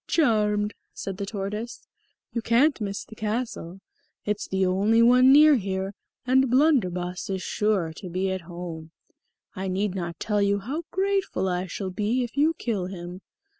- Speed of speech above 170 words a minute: No, average, 165 wpm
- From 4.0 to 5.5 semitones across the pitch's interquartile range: Yes, average, 4.3 semitones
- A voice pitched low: No, high, 205 Hz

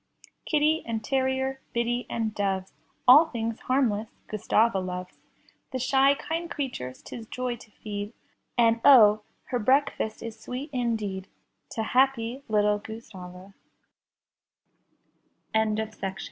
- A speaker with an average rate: No, slow, 105 wpm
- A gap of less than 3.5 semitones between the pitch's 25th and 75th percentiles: No, average, 4.0 semitones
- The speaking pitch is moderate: No, high, 230 Hz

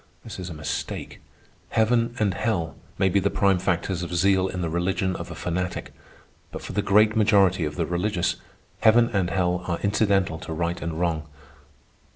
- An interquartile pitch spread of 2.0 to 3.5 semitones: Yes, average, 2.8 semitones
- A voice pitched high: No, very low, 90 Hz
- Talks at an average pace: Yes, average, 185 wpm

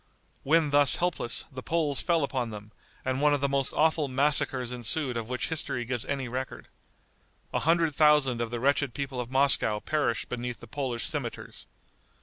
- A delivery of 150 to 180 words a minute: Yes, average, 175 wpm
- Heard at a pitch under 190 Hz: Yes, low, 135 Hz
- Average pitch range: Yes, average, 3.2 semitones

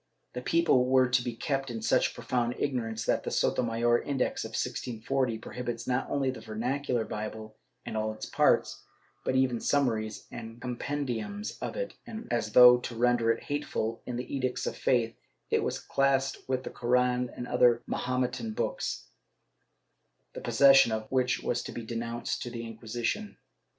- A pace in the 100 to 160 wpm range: No, average, 170 wpm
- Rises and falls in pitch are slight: Yes, narrow, 2.3 semitones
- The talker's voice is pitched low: Yes, low, 125 Hz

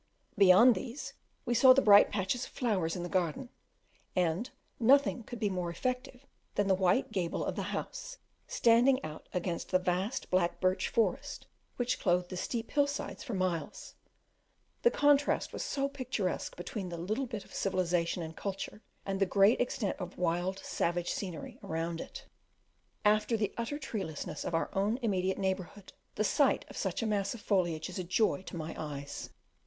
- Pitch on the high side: Yes, high, 195 Hz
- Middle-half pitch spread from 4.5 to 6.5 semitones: Yes, average, 5.2 semitones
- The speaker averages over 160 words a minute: Yes, average, 175 wpm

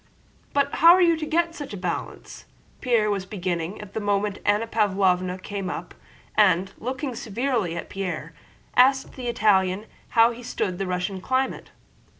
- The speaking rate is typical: Yes, average, 150 wpm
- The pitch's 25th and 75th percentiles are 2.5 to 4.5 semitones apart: No, average, 5.3 semitones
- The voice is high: Yes, high, 210 Hz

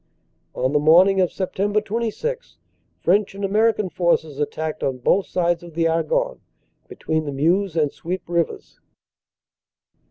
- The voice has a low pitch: No, medium, 175 Hz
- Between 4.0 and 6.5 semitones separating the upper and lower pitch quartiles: Yes, average, 4.3 semitones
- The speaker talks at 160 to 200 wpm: No, slow, 135 wpm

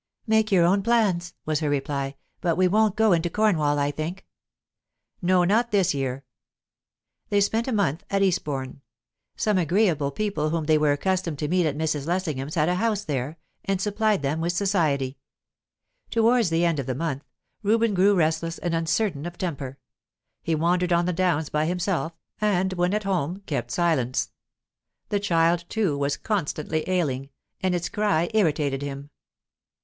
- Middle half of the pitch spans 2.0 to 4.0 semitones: No, average, 4.8 semitones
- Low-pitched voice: No, medium, 170 Hz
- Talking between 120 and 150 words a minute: No, average, 165 wpm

